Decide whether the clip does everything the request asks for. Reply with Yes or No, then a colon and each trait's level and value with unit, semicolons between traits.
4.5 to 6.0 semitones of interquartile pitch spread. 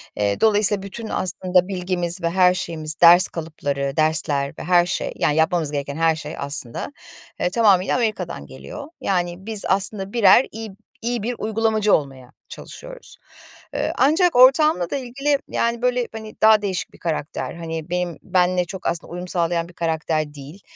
Yes: average, 5.2 semitones